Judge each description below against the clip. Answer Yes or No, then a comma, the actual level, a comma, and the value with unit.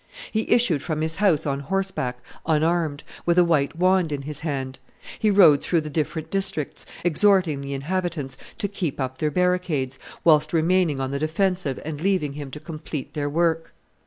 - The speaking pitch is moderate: Yes, medium, 160 Hz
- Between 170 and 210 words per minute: Yes, average, 175 wpm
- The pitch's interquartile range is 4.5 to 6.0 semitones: No, average, 3.9 semitones